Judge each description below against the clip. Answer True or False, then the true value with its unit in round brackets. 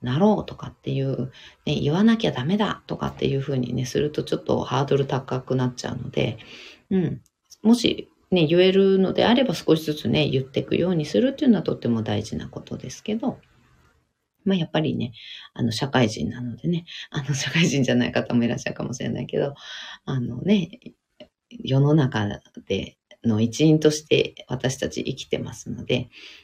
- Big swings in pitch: True (6.1 semitones)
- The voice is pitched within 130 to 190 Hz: True (140 Hz)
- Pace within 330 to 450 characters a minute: True (365 characters per minute)